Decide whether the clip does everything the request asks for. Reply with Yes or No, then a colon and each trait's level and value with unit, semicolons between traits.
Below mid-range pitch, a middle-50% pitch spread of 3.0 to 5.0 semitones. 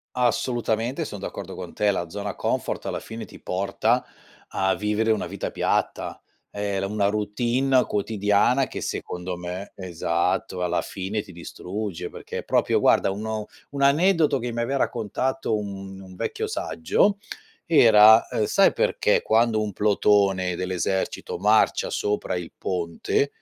Yes: low, 105 Hz; average, 3.5 semitones